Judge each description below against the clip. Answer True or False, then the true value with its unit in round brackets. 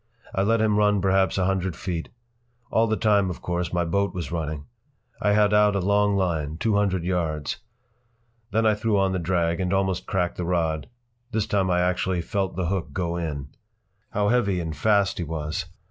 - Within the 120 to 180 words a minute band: False (190 wpm)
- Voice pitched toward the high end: False (95 Hz)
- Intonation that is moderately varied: True (3.2 semitones)